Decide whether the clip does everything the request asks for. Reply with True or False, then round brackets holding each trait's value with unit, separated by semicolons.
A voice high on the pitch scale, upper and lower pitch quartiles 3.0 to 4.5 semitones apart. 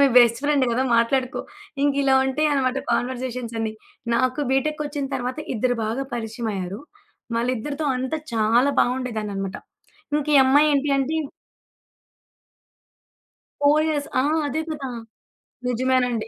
True (255 Hz; 3.3 semitones)